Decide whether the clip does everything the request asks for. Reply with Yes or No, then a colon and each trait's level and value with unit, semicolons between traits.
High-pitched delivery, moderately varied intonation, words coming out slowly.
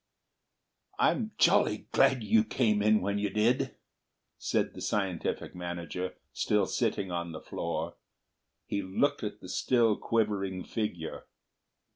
No: low, 105 Hz; average, 3.4 semitones; slow, 125 wpm